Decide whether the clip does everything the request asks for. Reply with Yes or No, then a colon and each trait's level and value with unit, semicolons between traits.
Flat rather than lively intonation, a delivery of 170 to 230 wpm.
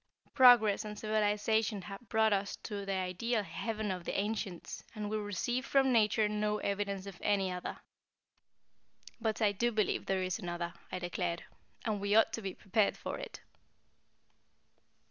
No: narrow, 2.2 semitones; average, 160 wpm